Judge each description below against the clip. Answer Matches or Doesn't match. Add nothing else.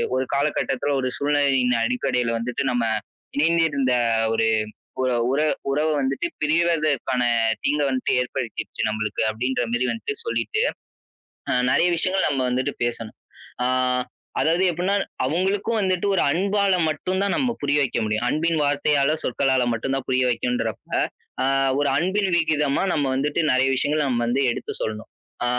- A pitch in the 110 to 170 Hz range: Matches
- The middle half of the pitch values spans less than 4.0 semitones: Doesn't match